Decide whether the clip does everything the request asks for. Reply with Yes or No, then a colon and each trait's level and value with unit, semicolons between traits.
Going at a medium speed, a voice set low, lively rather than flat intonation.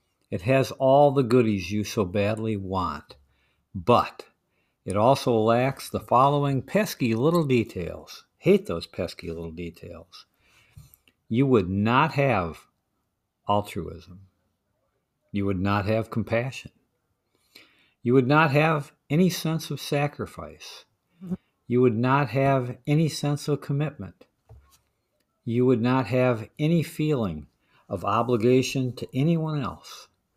No: slow, 120 wpm; low, 125 Hz; wide, 5.9 semitones